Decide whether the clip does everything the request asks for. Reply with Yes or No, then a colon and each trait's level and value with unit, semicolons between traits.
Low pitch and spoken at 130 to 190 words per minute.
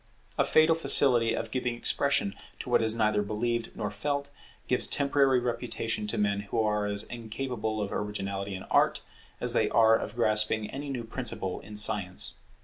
Yes: low, 110 Hz; average, 170 wpm